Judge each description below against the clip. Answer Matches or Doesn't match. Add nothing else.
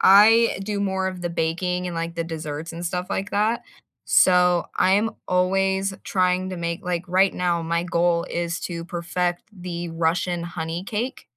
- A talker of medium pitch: Matches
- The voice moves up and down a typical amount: Doesn't match